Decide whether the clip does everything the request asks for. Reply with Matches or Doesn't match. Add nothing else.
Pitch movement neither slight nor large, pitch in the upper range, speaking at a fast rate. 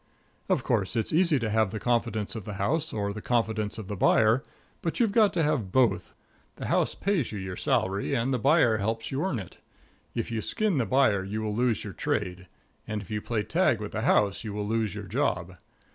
Doesn't match